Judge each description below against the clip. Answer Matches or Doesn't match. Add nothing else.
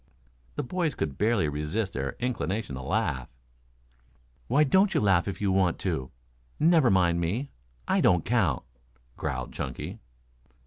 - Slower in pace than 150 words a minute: Matches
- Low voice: Matches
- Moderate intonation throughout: Doesn't match